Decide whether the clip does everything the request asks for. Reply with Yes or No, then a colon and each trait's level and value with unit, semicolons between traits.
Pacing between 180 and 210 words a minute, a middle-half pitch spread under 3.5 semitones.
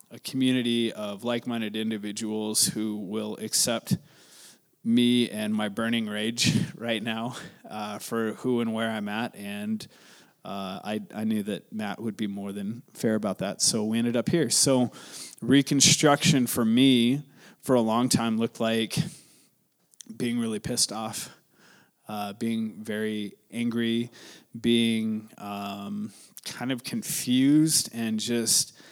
No: average, 140 wpm; narrow, 2.5 semitones